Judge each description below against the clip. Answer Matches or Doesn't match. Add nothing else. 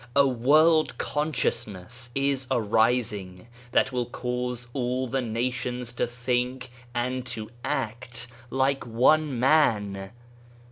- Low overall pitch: Matches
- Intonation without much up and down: Matches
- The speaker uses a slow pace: Matches